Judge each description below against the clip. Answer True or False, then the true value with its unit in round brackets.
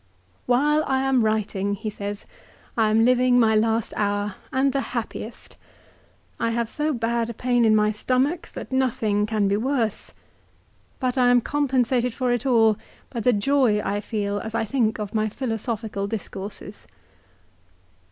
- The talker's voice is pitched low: False (230 Hz)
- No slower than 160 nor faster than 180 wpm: True (165 wpm)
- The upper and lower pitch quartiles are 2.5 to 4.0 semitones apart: True (3.1 semitones)